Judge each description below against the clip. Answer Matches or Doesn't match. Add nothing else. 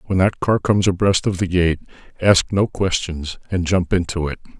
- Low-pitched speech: Matches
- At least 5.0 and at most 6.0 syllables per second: Matches